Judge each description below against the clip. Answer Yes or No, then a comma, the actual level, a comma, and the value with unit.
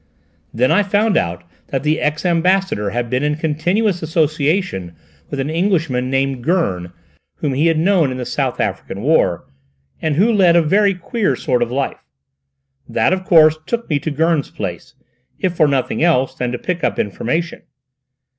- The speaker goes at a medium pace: Yes, average, 175 wpm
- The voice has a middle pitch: Yes, medium, 155 Hz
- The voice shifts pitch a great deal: Yes, wide, 5.7 semitones